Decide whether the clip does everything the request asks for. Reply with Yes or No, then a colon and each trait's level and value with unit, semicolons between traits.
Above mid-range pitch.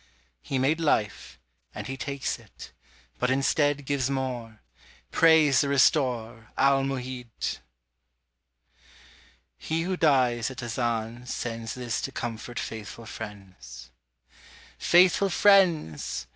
No: low, 130 Hz